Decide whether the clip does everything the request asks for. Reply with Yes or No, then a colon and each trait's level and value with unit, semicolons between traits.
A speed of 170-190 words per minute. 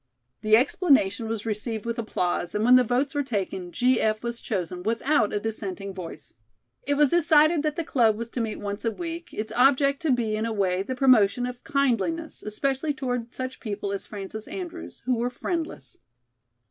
Yes: average, 185 wpm